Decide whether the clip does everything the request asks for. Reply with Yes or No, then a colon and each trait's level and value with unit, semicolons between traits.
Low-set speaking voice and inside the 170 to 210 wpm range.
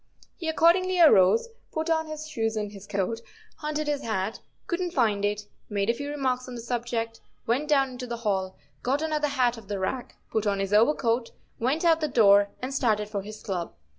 No: high, 240 Hz; average, 200 wpm